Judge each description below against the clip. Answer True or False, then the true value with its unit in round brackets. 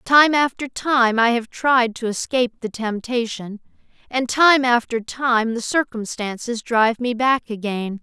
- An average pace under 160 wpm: True (150 wpm)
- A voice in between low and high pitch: False (240 Hz)